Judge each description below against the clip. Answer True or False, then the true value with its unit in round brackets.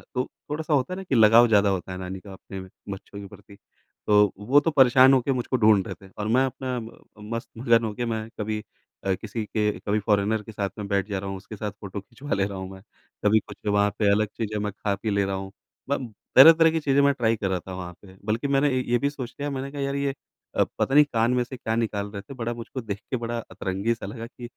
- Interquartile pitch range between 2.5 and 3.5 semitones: False (4.1 semitones)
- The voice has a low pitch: True (110 Hz)